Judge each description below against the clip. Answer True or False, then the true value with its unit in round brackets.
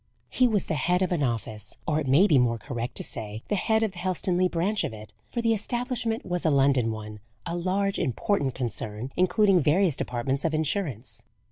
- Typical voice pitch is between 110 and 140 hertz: False (160 Hz)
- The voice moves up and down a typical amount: False (7.9 semitones)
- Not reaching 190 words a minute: False (205 wpm)